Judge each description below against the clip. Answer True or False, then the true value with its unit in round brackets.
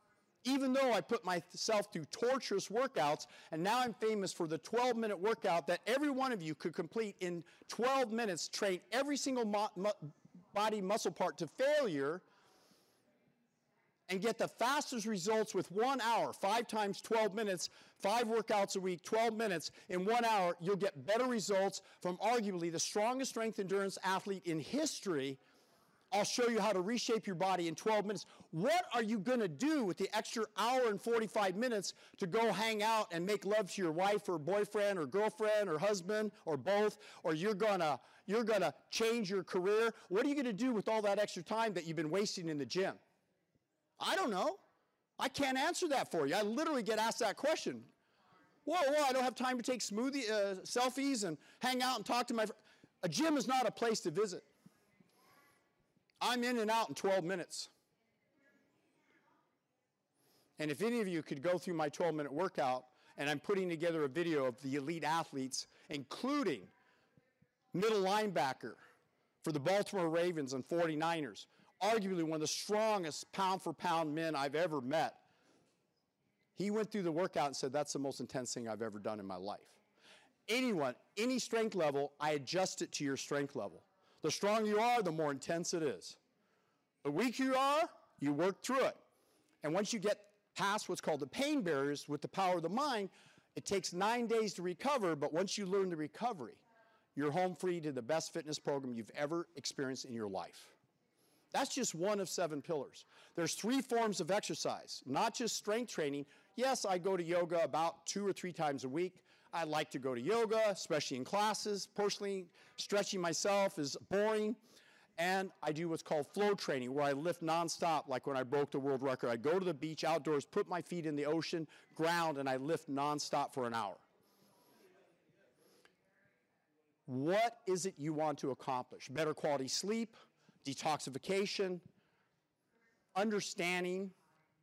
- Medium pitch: False (195 Hz)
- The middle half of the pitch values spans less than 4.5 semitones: False (5.6 semitones)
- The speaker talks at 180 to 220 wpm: True (185 wpm)